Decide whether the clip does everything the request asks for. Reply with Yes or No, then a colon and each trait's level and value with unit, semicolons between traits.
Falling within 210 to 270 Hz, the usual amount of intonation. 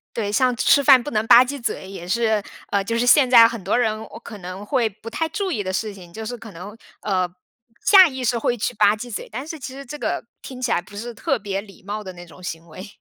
Yes: high, 220 Hz; average, 4.0 semitones